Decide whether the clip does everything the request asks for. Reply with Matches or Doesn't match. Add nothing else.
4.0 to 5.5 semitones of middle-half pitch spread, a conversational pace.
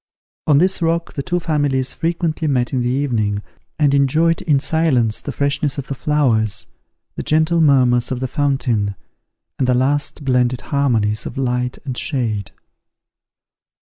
Doesn't match